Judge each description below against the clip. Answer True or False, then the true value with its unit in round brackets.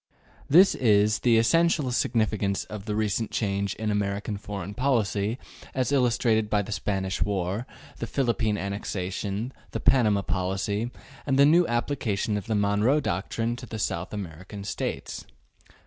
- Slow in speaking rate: False (145 wpm)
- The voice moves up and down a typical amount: True (3.1 semitones)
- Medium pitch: False (105 Hz)